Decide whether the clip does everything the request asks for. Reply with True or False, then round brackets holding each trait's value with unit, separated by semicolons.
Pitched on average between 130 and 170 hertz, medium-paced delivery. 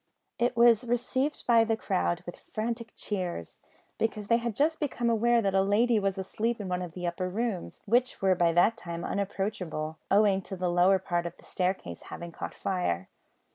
False (195 Hz; 190 wpm)